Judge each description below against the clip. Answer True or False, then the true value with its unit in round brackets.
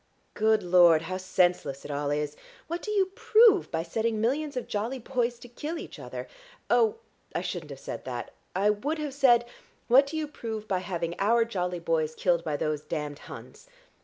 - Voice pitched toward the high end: True (215 Hz)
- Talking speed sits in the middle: True (190 wpm)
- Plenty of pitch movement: True (8.0 semitones)